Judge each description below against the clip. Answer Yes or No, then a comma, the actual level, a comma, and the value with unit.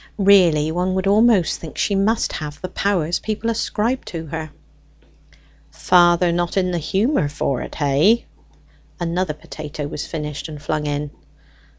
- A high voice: No, medium, 175 Hz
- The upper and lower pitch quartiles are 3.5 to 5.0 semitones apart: Yes, average, 4.5 semitones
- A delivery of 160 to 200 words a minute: No, average, 145 wpm